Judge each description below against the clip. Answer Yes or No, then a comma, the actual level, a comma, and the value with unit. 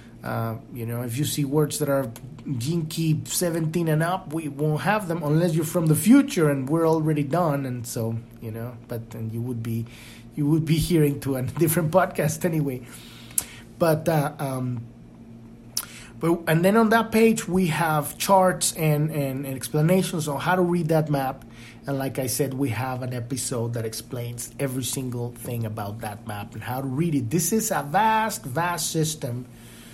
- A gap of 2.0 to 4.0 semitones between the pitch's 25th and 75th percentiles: No, wide, 5.6 semitones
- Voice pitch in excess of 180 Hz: No, medium, 140 Hz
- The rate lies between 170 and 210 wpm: Yes, average, 185 wpm